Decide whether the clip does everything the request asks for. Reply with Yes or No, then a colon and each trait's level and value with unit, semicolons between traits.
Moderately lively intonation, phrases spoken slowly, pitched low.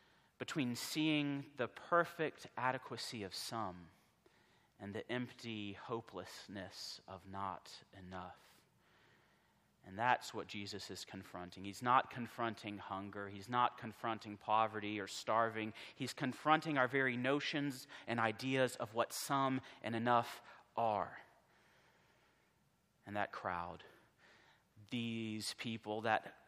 Yes: average, 3.8 semitones; slow, 110 wpm; low, 115 Hz